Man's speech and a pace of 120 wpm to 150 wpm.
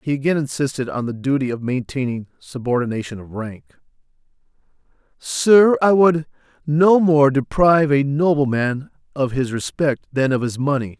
Yes: male; average, 140 wpm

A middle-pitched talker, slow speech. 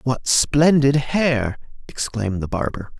No: low, 130 Hz; slow, 120 wpm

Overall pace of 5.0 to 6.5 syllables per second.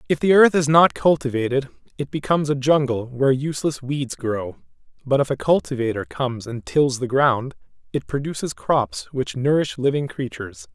Yes: 5.3 syllables/s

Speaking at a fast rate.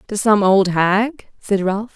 No: average, 185 wpm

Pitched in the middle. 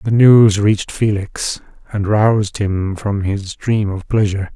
No: low, 100 Hz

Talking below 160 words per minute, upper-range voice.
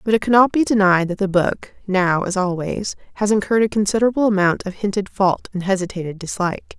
No: average, 195 wpm; high, 195 Hz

